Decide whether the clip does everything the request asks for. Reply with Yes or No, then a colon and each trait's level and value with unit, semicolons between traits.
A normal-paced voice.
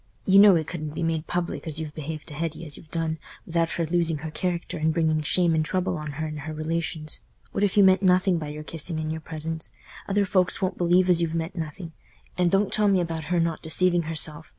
No: fast, 245 wpm